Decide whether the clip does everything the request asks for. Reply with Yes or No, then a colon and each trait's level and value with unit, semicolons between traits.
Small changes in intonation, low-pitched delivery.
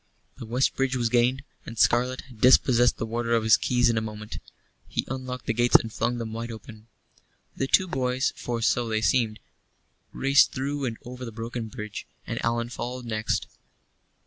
Yes: narrow, 2.1 semitones; low, 120 Hz